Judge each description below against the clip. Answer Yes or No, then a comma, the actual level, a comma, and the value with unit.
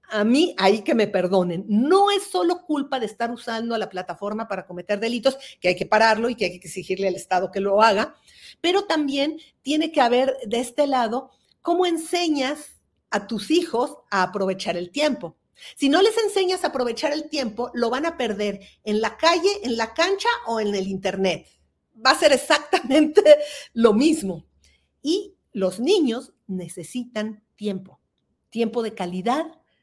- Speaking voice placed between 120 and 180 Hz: No, high, 240 Hz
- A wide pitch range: Yes, wide, 6.8 semitones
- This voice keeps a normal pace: Yes, average, 170 wpm